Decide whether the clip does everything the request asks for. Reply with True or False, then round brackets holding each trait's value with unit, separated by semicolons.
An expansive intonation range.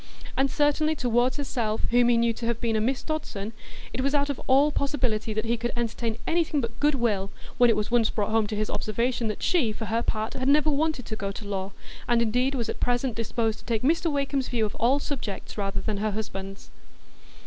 False (3.9 semitones)